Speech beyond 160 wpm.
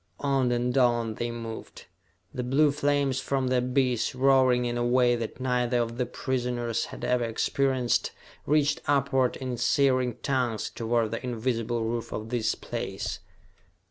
No: average, 150 wpm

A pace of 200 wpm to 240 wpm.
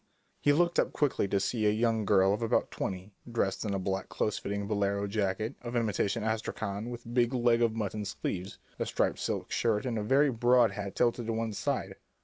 Yes: fast, 205 wpm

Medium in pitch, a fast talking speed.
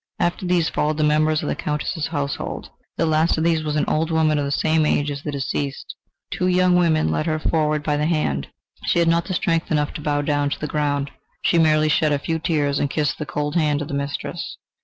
Yes: medium, 155 Hz; fast, 235 wpm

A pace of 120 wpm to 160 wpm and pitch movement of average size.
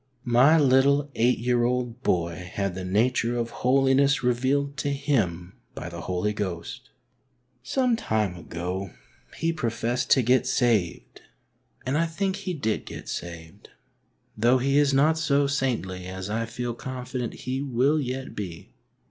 No: average, 150 wpm; wide, 5.7 semitones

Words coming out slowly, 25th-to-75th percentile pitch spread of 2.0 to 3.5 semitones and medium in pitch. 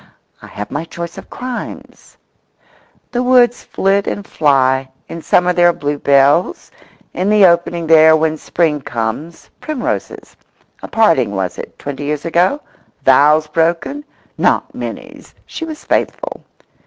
No: slow, 130 wpm; average, 5.2 semitones; medium, 165 Hz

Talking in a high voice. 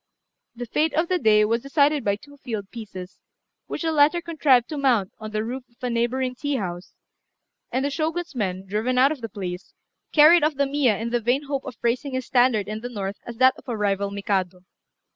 Yes: high, 245 Hz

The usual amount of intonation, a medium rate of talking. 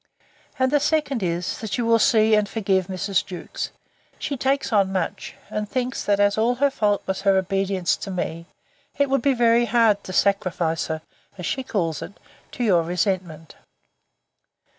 Yes: average, 4.4 semitones; average, 175 wpm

